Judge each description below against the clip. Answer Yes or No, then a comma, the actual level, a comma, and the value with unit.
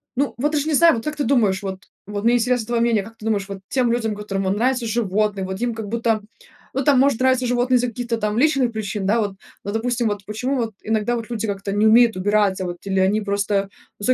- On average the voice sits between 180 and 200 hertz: No, high, 225 Hz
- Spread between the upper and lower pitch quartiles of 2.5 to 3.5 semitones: Yes, average, 3.2 semitones